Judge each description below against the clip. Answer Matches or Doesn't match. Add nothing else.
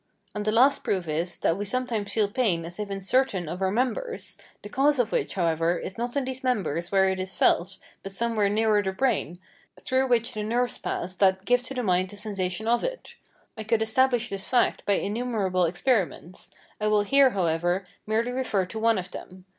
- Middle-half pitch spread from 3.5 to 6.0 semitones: Matches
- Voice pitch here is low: Doesn't match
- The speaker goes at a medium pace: Doesn't match